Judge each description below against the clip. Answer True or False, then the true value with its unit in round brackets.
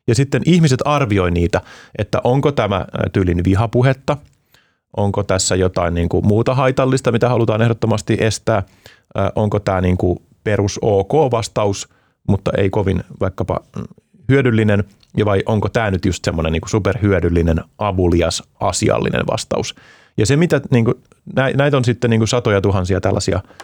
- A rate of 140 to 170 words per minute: True (145 wpm)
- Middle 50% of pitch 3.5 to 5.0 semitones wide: True (4.2 semitones)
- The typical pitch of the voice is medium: False (105 Hz)